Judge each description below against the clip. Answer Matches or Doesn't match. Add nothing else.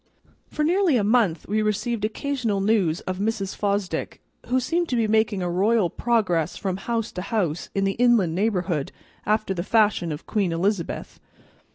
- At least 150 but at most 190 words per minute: Matches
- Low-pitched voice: Doesn't match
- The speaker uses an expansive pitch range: Doesn't match